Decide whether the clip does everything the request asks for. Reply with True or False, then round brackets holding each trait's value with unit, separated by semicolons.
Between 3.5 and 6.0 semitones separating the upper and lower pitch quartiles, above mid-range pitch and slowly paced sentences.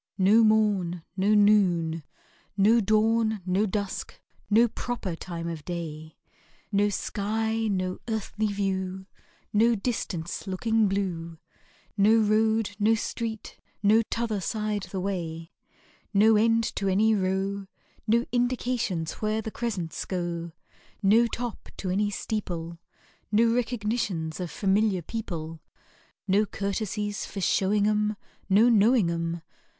False (3.1 semitones; 205 Hz; 120 wpm)